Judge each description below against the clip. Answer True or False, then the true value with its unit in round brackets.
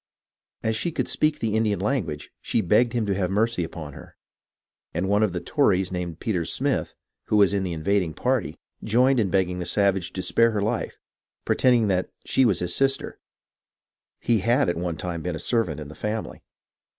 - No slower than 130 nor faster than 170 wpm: False (190 wpm)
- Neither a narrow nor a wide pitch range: True (4.5 semitones)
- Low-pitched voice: True (100 Hz)